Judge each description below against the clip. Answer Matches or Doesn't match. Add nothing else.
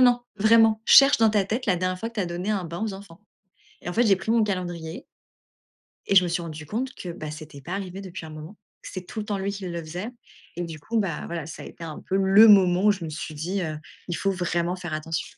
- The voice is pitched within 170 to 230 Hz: Matches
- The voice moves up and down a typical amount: Matches